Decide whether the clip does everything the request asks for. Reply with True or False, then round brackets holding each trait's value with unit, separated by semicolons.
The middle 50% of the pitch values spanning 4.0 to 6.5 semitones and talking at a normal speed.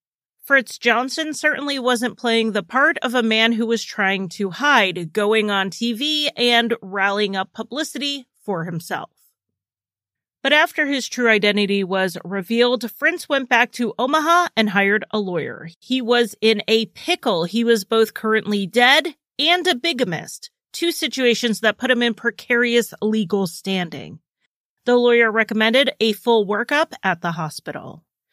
True (4.5 semitones; 150 wpm)